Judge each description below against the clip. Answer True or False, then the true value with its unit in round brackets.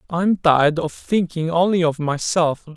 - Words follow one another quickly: False (150 wpm)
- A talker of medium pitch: True (165 Hz)